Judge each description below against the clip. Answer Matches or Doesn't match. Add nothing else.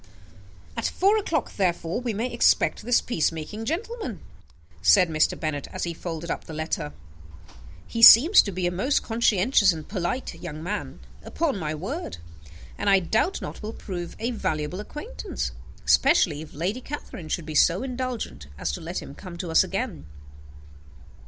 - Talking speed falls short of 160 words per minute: Doesn't match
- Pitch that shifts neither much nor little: Doesn't match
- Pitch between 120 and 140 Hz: Doesn't match